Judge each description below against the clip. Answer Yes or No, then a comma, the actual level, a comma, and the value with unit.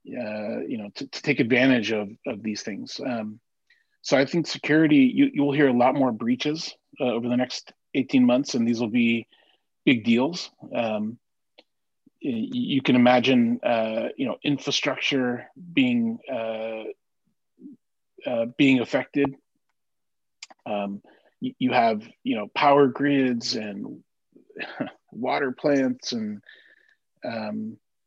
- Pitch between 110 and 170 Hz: Yes, medium, 140 Hz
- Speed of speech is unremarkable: No, slow, 130 wpm